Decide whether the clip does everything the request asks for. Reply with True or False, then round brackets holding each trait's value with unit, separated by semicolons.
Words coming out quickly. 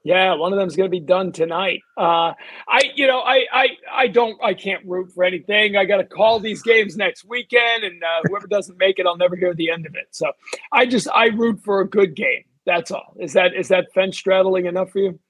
True (245 wpm)